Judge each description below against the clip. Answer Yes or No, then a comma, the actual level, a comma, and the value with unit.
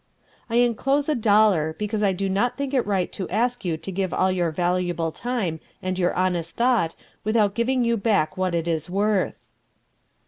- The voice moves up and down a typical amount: Yes, average, 4.8 semitones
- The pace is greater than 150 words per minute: Yes, average, 185 wpm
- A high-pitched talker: Yes, high, 195 Hz